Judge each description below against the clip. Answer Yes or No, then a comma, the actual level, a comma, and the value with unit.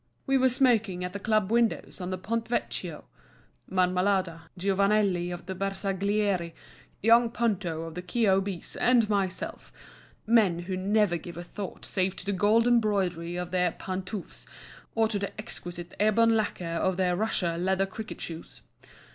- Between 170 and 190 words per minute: No, average, 145 wpm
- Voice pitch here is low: No, high, 195 Hz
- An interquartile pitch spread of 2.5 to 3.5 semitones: Yes, average, 3.2 semitones